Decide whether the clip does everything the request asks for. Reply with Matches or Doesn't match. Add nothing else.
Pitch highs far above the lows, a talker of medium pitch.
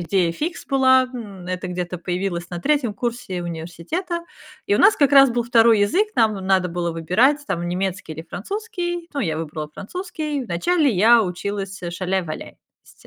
Doesn't match